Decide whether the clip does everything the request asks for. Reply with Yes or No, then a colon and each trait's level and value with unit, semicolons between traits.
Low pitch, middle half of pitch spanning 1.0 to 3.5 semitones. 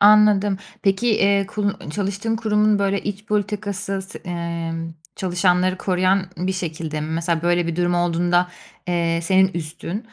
No: medium, 185 Hz; average, 2.9 semitones